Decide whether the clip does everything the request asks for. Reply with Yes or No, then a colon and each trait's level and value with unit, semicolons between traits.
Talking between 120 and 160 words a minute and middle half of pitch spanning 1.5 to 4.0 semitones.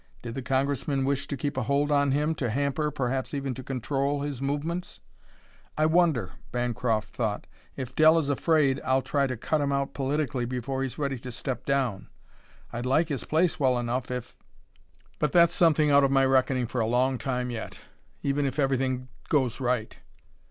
No: average, 185 wpm; narrow, 2.4 semitones